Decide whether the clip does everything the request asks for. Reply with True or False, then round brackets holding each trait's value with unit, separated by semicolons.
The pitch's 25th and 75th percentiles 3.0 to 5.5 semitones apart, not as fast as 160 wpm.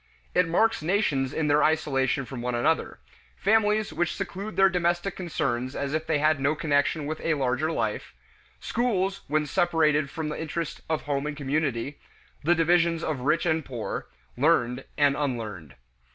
False (3.6 semitones; 165 wpm)